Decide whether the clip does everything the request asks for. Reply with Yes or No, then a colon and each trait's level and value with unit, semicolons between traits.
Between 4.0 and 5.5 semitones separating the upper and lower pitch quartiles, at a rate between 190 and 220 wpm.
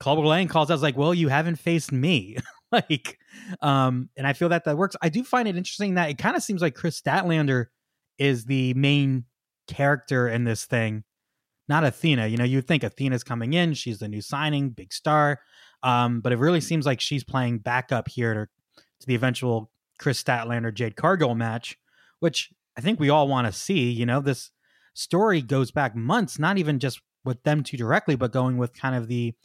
Yes: average, 4.3 semitones; average, 200 wpm